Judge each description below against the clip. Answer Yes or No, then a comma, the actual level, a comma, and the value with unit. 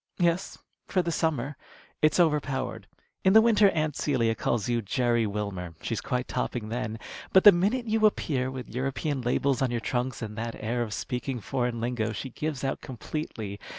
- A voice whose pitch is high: No, low, 125 Hz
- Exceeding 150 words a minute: Yes, average, 185 wpm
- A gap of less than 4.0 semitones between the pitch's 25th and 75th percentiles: No, average, 5.0 semitones